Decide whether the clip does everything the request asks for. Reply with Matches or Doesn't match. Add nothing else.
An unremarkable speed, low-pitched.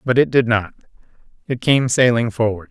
Matches